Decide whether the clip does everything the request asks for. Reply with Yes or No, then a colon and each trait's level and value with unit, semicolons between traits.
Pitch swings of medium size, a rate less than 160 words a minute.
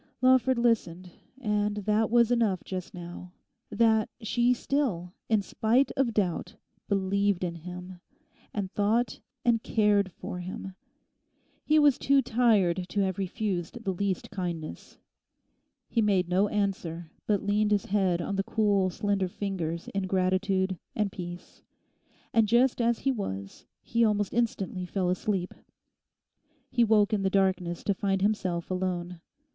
Yes: average, 3.3 semitones; average, 140 wpm